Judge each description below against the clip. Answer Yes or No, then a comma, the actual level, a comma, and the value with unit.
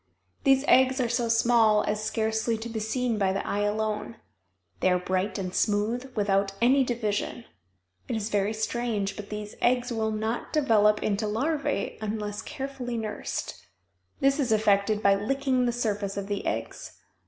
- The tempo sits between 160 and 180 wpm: Yes, average, 165 wpm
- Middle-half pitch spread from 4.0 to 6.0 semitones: No, average, 2.7 semitones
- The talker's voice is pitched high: Yes, high, 220 Hz